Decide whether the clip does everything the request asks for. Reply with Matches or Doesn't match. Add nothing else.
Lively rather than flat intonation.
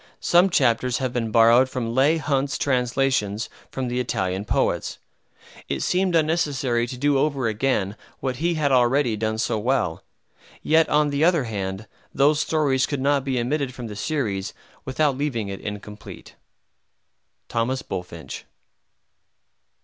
Doesn't match